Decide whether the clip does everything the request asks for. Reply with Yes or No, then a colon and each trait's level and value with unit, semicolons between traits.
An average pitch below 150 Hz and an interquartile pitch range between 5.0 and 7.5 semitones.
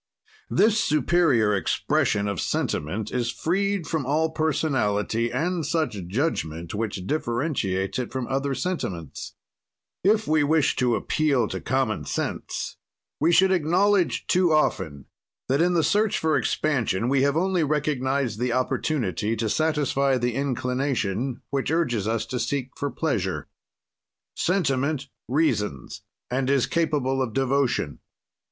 Yes: low, 135 Hz; wide, 5.4 semitones